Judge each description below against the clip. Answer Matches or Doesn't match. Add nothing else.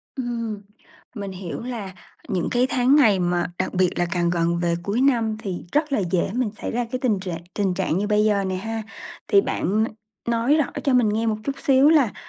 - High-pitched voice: Matches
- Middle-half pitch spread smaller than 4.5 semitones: Doesn't match